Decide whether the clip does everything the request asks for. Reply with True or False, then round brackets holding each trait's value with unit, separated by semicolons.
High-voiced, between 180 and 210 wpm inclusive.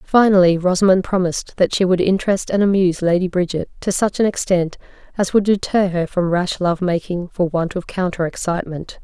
False (180 Hz; 185 wpm)